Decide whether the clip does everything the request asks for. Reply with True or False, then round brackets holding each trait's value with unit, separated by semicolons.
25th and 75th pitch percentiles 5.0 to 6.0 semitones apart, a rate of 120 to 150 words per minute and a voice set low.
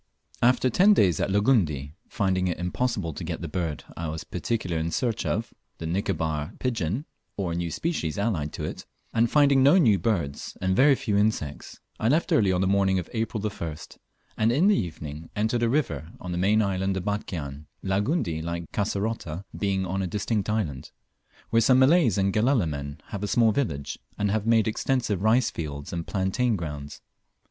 False (5.5 semitones; 190 wpm; 100 Hz)